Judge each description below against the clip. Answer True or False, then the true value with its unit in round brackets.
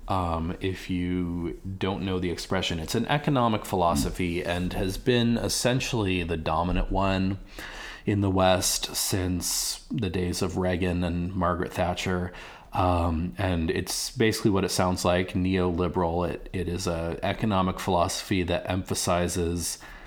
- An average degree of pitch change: False (1.6 semitones)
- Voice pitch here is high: False (90 Hz)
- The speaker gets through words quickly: False (140 wpm)